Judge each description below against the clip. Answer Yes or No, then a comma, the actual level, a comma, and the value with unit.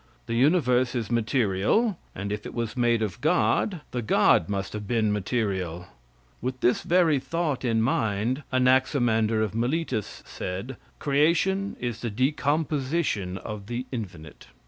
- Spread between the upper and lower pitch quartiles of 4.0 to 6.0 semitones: Yes, average, 4.7 semitones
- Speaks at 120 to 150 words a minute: Yes, average, 145 wpm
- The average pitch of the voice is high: No, low, 120 Hz